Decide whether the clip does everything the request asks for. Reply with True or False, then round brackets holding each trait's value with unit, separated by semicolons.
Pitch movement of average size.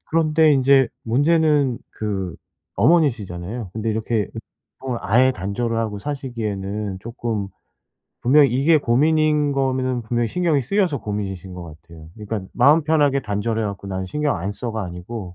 False (5.7 semitones)